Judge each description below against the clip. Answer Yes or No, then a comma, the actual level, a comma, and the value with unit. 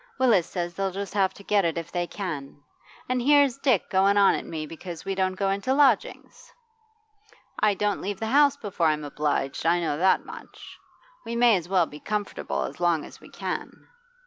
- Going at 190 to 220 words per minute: Yes, average, 200 wpm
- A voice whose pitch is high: Yes, high, 195 Hz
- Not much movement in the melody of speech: No, average, 4.0 semitones